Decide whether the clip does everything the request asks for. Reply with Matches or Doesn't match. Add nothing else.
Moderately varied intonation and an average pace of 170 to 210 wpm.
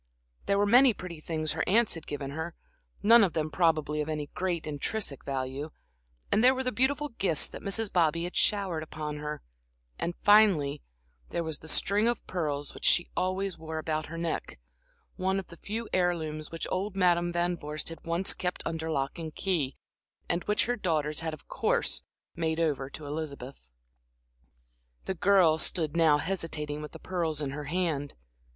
Matches